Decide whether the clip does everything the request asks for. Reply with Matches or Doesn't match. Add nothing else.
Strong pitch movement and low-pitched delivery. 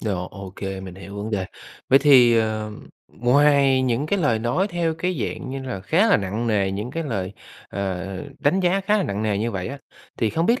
Matches